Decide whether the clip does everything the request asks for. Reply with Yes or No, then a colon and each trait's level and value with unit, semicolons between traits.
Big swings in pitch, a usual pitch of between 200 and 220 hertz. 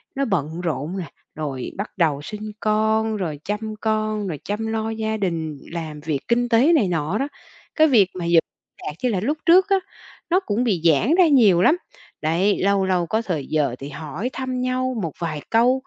Yes: wide, 6.0 semitones; high, 205 Hz